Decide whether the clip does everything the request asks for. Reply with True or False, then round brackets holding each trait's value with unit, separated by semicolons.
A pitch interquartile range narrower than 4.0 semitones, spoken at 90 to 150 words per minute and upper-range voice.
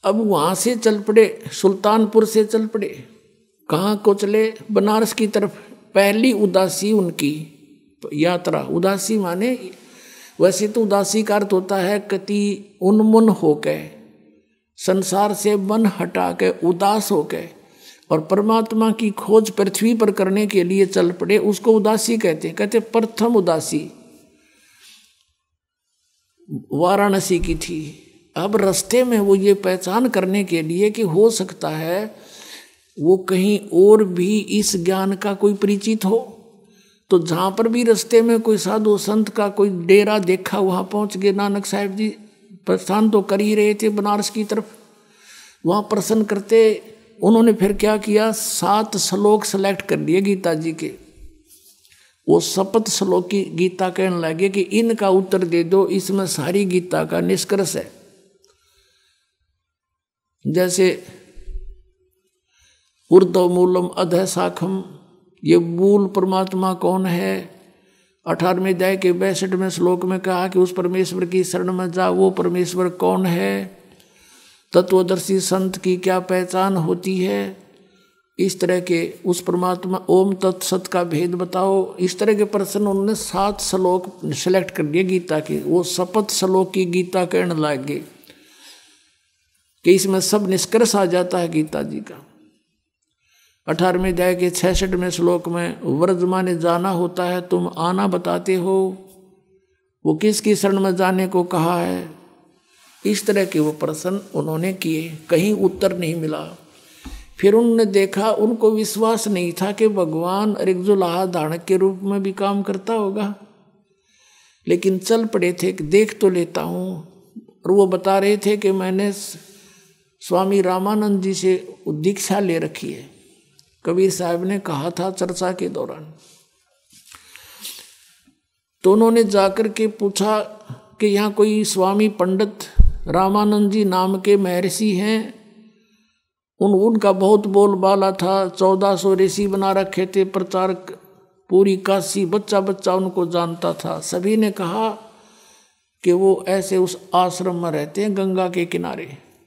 True (2.4 semitones; 140 wpm; 195 Hz)